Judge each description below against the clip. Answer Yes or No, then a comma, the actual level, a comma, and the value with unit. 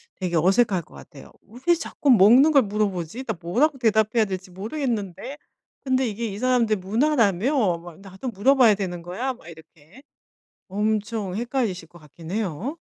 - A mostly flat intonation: No, average, 5.3 semitones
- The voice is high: Yes, high, 210 Hz